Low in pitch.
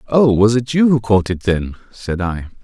Yes: low, 110 Hz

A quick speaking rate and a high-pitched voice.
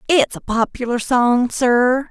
No: average, 145 wpm; very high, 250 Hz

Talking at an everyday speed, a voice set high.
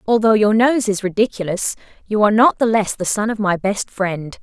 No: fast, 215 wpm; high, 210 Hz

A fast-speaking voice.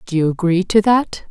Yes: fast, 230 wpm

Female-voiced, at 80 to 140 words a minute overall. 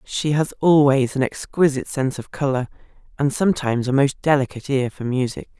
No: female; average, 170 wpm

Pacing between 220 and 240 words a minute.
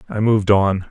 No: average, 200 wpm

